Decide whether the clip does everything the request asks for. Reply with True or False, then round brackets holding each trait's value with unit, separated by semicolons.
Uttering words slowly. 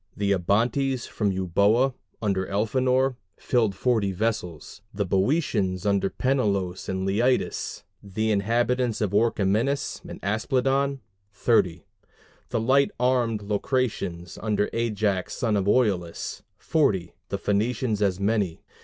True (120 wpm)